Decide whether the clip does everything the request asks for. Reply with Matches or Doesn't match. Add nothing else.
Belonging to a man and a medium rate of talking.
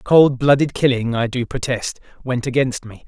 Matches